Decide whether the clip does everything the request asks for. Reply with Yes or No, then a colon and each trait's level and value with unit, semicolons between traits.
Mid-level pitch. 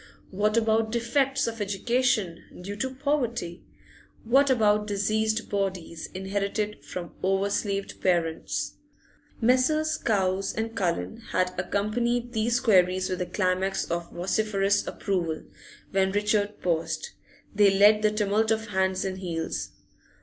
No: high, 205 Hz